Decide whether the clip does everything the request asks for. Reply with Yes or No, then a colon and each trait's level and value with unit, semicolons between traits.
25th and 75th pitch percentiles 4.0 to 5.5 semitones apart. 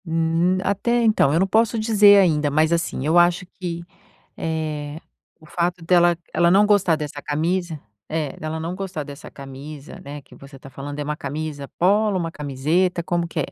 No: average, 3.5 semitones